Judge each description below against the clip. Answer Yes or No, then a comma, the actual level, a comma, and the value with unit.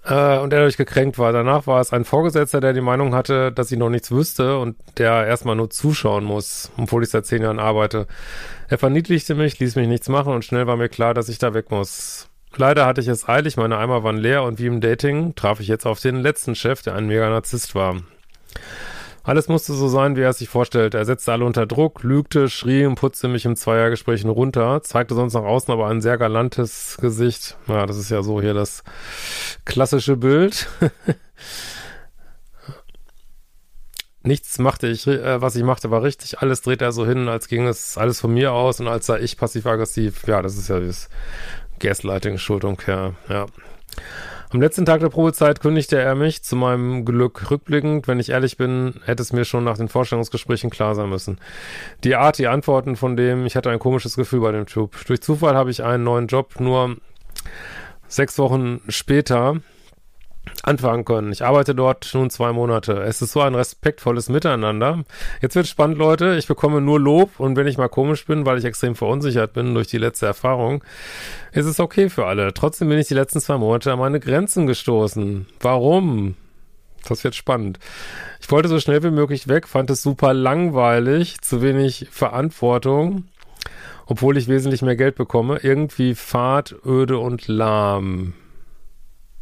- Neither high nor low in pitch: No, low, 125 Hz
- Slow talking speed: No, average, 185 wpm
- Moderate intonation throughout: Yes, average, 3.3 semitones